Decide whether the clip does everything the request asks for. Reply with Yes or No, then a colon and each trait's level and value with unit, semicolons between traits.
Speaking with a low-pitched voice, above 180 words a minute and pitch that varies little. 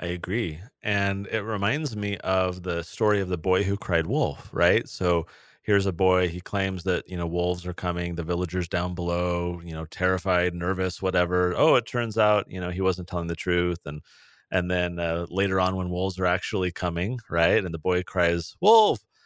Yes: very low, 90 Hz; fast, 205 wpm; narrow, 1.7 semitones